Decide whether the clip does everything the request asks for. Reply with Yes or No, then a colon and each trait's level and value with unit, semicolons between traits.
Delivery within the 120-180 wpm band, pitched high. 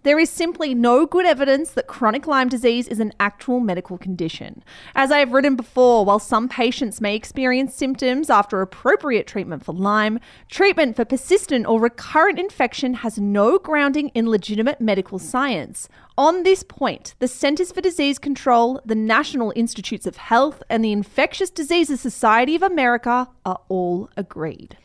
Yes: average, 160 wpm; very high, 250 Hz